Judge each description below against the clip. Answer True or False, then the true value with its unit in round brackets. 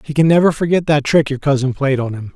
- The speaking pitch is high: False (145 Hz)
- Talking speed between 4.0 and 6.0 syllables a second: False (6.2 syllables/s)